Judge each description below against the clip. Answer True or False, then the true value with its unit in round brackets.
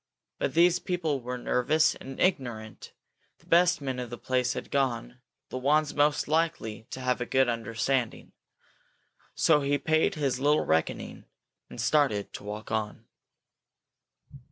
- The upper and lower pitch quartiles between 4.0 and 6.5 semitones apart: True (4.3 semitones)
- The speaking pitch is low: True (130 Hz)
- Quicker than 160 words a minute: False (145 wpm)